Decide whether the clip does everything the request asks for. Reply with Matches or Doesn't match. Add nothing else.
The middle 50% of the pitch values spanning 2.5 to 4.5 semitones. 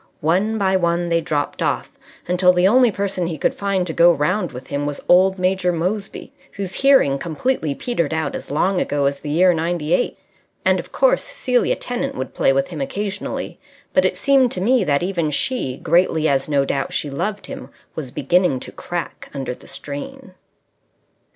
Doesn't match